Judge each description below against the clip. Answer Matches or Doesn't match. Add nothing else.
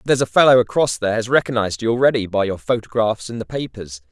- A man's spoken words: Matches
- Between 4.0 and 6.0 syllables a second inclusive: Doesn't match